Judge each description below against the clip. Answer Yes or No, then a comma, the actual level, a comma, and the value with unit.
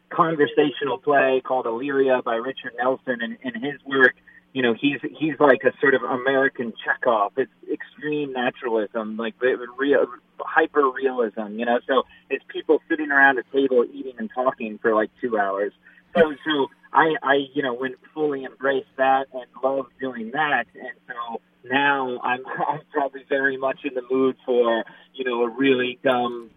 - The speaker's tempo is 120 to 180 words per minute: Yes, average, 165 wpm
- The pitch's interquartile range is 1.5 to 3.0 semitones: Yes, narrow, 2.4 semitones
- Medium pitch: No, low, 130 Hz